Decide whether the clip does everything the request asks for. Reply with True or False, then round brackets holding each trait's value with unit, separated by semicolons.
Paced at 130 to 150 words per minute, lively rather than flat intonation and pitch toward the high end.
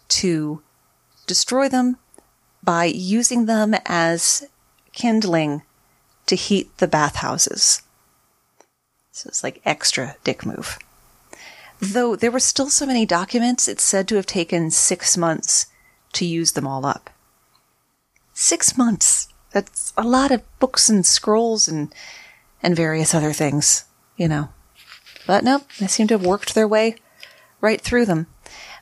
True (135 wpm; 6.1 semitones; 195 Hz)